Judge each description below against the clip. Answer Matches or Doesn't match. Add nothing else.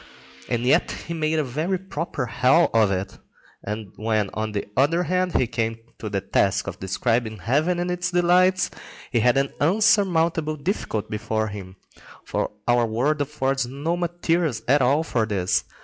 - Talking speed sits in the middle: Matches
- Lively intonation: Matches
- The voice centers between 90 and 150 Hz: Matches